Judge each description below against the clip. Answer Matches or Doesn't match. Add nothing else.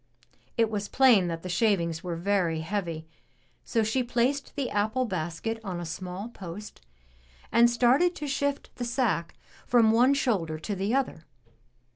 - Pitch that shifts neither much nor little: Doesn't match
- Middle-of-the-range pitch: Doesn't match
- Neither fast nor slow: Matches